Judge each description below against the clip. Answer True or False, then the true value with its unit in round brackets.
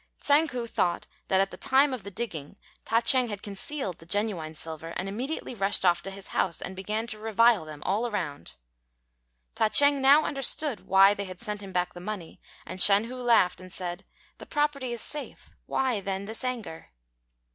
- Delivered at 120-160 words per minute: False (195 wpm)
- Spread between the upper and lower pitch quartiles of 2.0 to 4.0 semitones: False (4.8 semitones)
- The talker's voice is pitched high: True (205 Hz)